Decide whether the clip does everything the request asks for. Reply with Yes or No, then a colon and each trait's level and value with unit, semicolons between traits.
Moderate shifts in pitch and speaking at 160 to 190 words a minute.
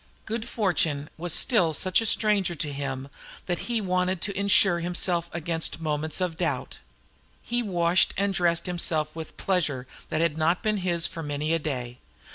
Yes: average, 3.2 semitones; average, 170 wpm